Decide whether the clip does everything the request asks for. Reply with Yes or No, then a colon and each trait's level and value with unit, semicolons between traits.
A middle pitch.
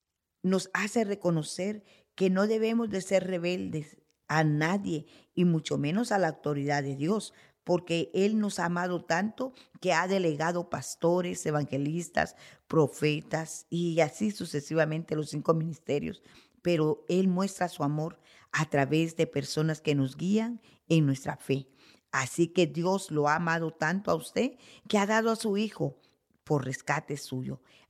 Yes: medium, 165 Hz